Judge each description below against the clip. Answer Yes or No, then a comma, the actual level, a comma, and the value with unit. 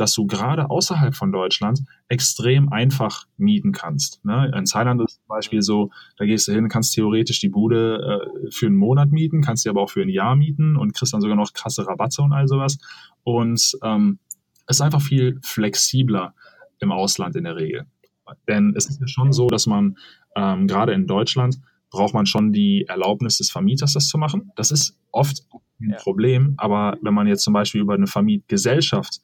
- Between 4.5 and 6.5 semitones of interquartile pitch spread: Yes, wide, 5.6 semitones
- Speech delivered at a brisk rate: Yes, fast, 200 wpm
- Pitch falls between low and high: No, low, 125 Hz